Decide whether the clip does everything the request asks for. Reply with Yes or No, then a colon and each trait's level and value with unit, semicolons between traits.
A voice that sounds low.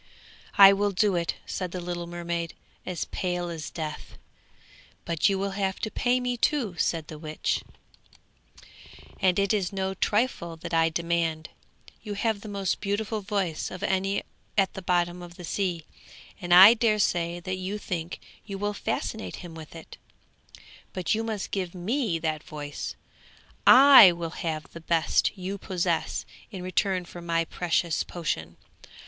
No: medium, 180 Hz